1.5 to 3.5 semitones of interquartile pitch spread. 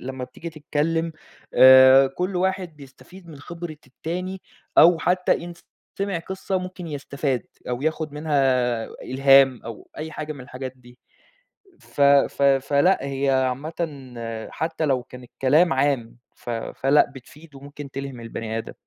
No: average, 4.0 semitones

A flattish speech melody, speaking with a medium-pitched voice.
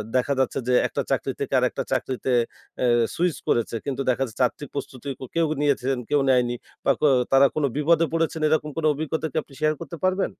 No: average, 3.3 semitones; medium, 145 Hz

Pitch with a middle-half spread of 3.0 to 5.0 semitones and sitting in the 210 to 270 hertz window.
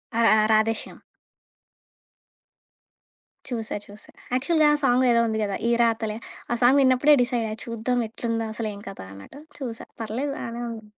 No: narrow, 2.5 semitones; high, 230 Hz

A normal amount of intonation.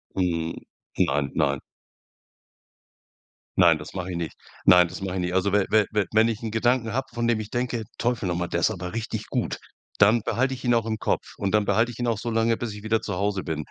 Yes: average, 4.0 semitones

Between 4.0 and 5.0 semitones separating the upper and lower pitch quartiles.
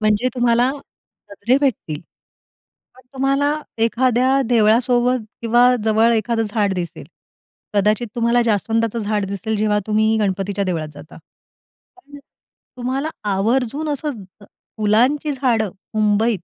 No: average, 3.4 semitones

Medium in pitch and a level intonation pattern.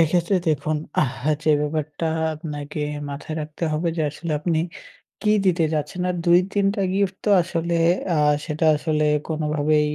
Yes: medium, 155 Hz; narrow, 2.3 semitones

